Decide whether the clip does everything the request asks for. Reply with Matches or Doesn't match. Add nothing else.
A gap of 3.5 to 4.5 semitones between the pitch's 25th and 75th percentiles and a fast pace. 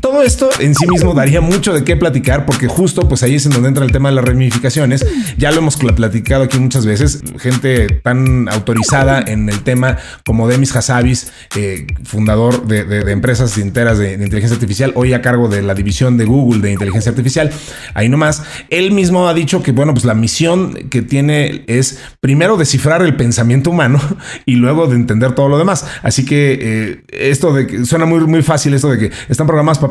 Matches